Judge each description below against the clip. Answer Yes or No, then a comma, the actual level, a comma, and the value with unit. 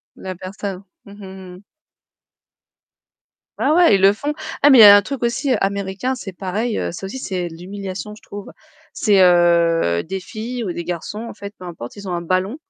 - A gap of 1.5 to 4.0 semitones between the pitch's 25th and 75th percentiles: Yes, average, 2.9 semitones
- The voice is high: Yes, high, 195 Hz